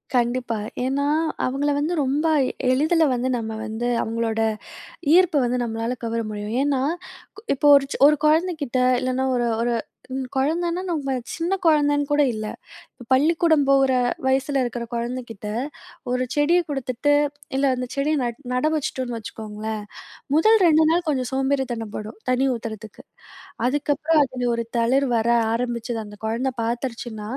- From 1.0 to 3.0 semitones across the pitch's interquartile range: No, average, 3.8 semitones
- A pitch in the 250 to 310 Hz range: Yes, very high, 255 Hz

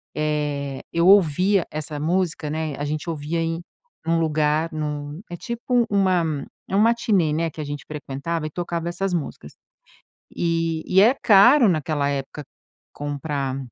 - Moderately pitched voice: Yes, medium, 160 Hz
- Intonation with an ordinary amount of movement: Yes, average, 3.5 semitones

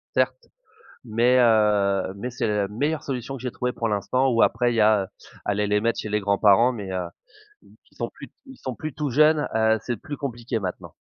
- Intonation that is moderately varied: Yes, average, 3.6 semitones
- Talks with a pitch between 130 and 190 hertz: No, low, 115 Hz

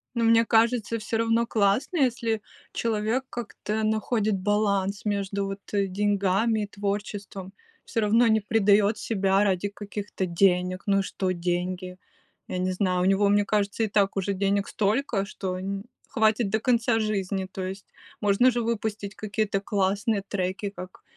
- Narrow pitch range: Yes, narrow, 2.1 semitones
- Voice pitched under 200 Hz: No, high, 205 Hz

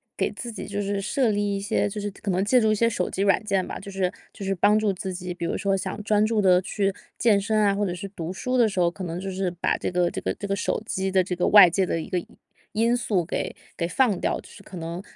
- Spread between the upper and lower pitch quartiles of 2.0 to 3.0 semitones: Yes, narrow, 2.4 semitones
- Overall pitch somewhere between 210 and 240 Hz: No, high, 195 Hz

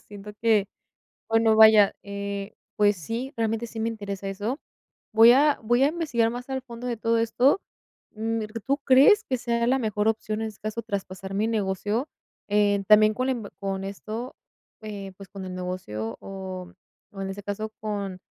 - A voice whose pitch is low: No, high, 215 Hz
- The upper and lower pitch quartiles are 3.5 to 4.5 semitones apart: No, average, 2.8 semitones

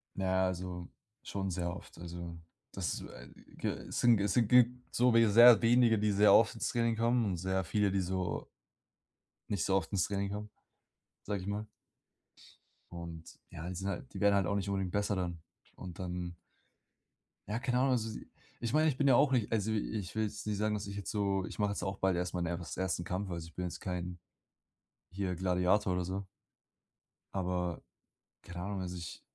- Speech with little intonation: No, average, 3.0 semitones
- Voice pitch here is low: Yes, very low, 95 Hz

